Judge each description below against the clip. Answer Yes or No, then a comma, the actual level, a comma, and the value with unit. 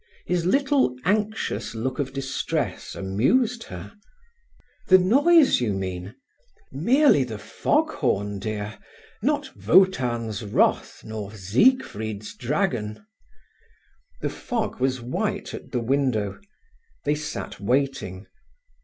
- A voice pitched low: Yes, low, 125 Hz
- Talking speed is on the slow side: Yes, slow, 100 wpm